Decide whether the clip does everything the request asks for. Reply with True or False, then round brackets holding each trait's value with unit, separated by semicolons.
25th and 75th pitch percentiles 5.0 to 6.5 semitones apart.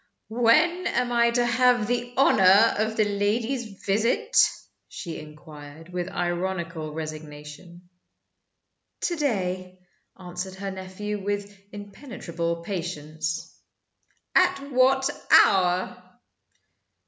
True (5.3 semitones)